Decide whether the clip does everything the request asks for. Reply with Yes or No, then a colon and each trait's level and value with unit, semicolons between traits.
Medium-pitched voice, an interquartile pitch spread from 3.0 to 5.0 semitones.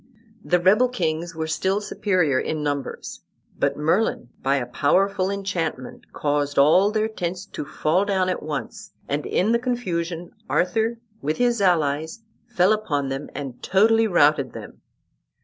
No: medium, 175 Hz; wide, 5.6 semitones